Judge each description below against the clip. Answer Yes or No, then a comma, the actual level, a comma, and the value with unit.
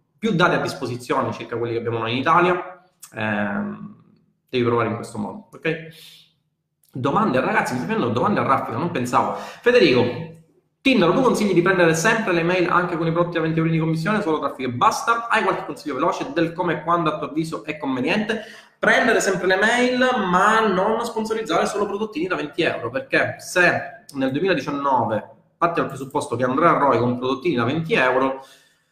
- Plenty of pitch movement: Yes, wide, 6.3 semitones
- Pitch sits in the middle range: Yes, medium, 170 Hz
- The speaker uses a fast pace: Yes, fast, 185 wpm